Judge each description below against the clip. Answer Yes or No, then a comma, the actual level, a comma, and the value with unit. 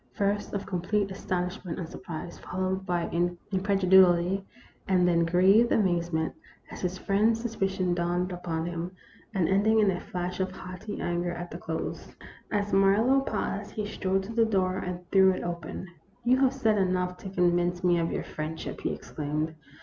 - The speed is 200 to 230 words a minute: No, average, 175 wpm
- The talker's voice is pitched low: No, medium, 185 Hz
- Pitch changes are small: Yes, narrow, 2.2 semitones